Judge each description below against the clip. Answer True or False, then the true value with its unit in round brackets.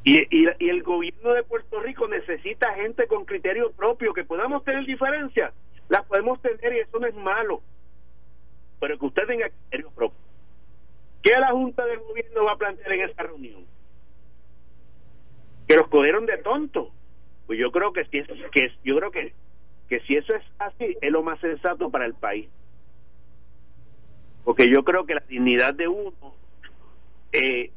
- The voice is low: False (160 Hz)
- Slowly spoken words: False (170 wpm)